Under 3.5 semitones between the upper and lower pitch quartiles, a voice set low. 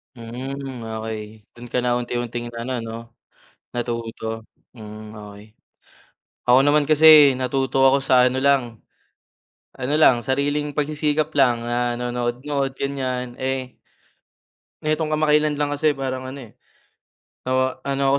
Yes: average, 2.7 semitones; low, 130 Hz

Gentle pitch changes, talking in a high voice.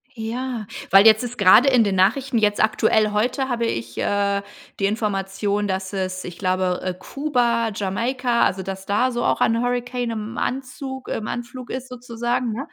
No: average, 3.7 semitones; high, 225 Hz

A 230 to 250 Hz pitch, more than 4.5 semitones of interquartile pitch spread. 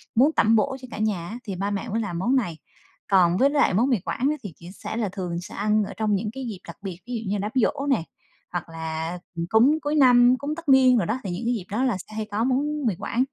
No: high, 220 Hz; average, 5.1 semitones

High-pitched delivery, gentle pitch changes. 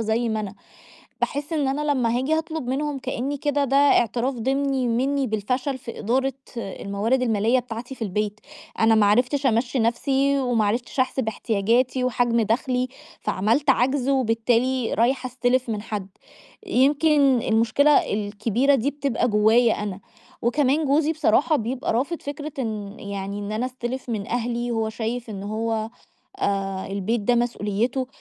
No: high, 245 Hz; average, 3.4 semitones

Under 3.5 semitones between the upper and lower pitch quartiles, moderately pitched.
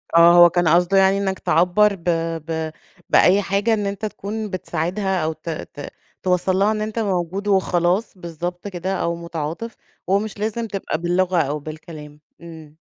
Yes: average, 3.0 semitones; medium, 180 Hz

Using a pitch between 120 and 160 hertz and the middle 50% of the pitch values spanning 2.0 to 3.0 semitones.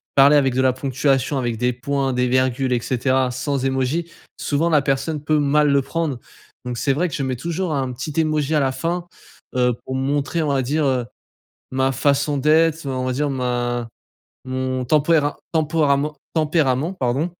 Yes: medium, 140 Hz; average, 2.7 semitones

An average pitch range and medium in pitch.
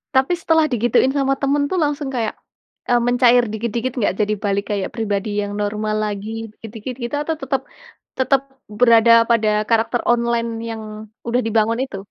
No: average, 3.5 semitones; high, 230 Hz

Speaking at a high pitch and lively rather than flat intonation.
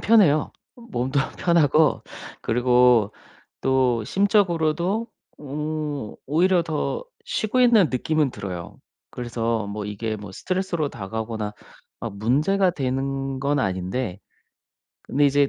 No: medium, 140 Hz; wide, 6.7 semitones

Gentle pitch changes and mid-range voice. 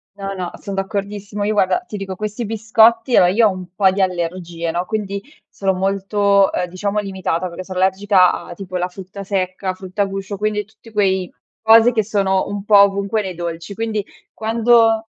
No: narrow, 2.1 semitones; high, 195 Hz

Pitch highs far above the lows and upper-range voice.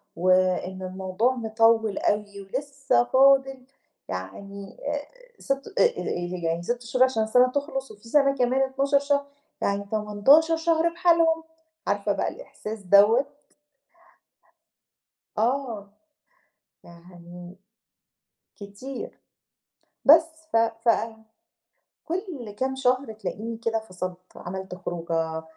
Yes: wide, 6.1 semitones; high, 225 Hz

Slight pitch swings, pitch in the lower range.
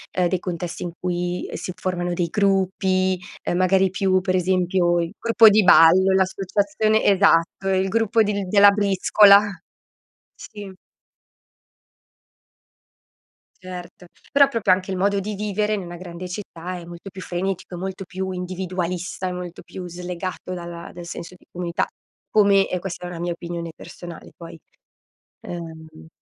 No: narrow, 1.8 semitones; medium, 185 Hz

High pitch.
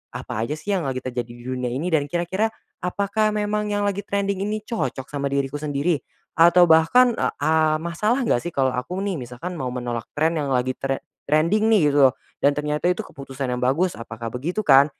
No: medium, 155 Hz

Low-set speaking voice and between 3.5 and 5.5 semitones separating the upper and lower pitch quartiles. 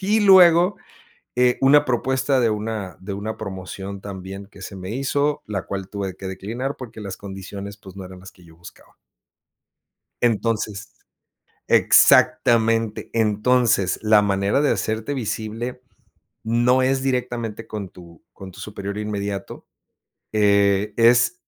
Yes: low, 105 Hz; average, 4.0 semitones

